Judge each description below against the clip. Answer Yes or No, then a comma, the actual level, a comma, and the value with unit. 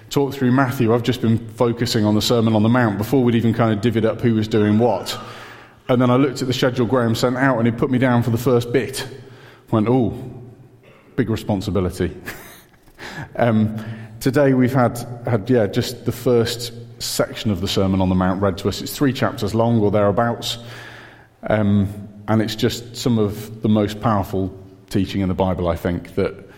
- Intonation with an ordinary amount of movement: Yes, average, 3.0 semitones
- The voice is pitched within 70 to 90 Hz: No, low, 115 Hz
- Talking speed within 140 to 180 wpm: No, average, 200 wpm